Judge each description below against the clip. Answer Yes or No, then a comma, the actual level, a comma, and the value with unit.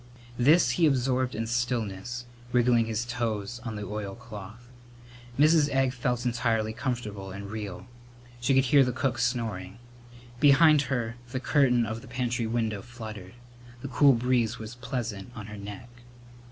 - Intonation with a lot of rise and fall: No, average, 2.7 semitones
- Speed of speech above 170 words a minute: No, average, 150 wpm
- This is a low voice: Yes, low, 120 Hz